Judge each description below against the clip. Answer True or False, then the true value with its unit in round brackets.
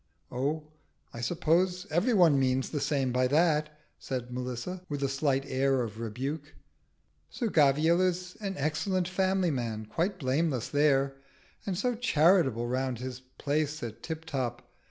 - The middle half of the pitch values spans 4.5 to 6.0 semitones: True (5.0 semitones)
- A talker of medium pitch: True (145 Hz)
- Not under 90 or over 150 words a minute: True (145 wpm)